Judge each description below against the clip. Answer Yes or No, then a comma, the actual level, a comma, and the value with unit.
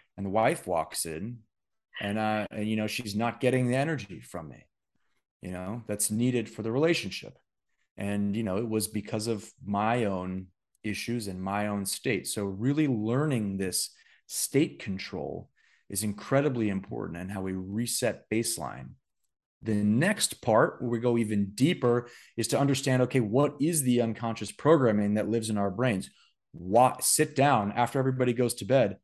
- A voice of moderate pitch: No, low, 110 Hz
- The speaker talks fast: No, average, 170 wpm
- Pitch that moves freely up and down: No, average, 3.6 semitones